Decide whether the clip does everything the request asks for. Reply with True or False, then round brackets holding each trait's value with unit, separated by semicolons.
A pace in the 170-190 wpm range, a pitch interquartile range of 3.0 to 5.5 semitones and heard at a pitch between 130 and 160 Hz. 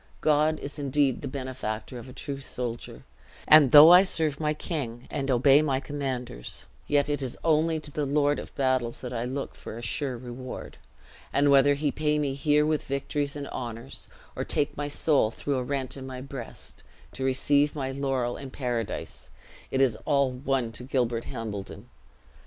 False (180 wpm; 2.6 semitones; 135 Hz)